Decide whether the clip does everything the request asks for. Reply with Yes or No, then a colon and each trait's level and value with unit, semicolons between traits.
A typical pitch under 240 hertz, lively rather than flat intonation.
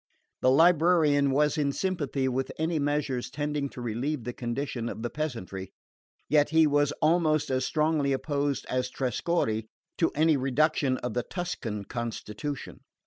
No: medium, 140 Hz; average, 3.5 semitones